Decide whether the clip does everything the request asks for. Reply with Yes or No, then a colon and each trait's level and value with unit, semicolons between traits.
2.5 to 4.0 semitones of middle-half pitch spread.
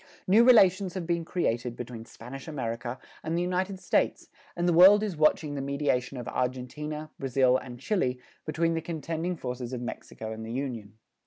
No: wide, 5.6 semitones